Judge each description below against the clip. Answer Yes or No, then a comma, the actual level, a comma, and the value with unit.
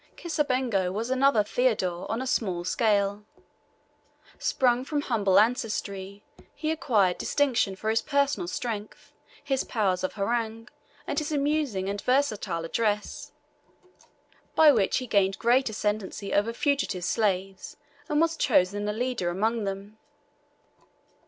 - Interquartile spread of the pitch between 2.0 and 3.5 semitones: No, average, 4.7 semitones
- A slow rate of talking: Yes, slow, 125 wpm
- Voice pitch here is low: No, high, 220 Hz